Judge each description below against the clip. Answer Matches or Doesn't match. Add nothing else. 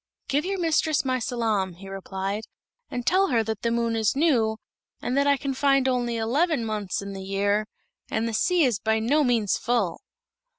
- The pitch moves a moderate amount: Matches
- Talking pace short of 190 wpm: Doesn't match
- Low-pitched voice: Doesn't match